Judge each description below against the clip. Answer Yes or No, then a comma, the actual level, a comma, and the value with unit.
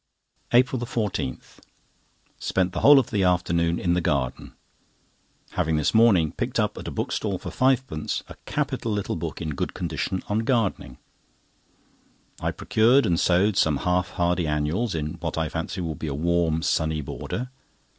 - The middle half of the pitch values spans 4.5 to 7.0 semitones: Yes, wide, 5.4 semitones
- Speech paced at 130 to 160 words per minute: Yes, average, 155 wpm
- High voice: No, very low, 90 Hz